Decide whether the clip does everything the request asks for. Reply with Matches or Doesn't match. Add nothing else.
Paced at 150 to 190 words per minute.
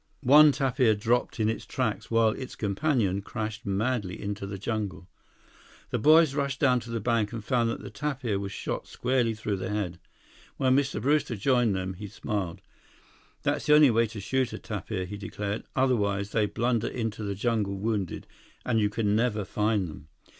Matches